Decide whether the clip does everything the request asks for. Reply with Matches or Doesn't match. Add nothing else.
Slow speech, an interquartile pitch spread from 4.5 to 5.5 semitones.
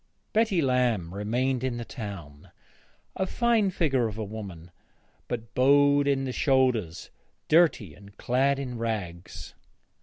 Matches